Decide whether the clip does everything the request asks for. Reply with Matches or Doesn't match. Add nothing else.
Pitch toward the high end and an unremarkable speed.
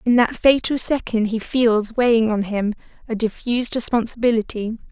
Matches